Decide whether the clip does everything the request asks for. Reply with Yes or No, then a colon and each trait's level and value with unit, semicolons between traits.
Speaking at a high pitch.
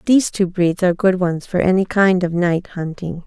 No: medium, 180 Hz